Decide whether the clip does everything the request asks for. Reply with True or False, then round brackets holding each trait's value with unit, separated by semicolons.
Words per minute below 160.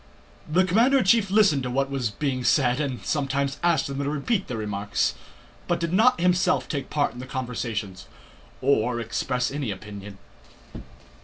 False (165 wpm)